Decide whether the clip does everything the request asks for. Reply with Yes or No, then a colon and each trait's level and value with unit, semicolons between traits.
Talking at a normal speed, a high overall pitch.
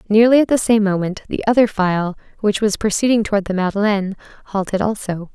Yes: average, 180 wpm; high, 205 Hz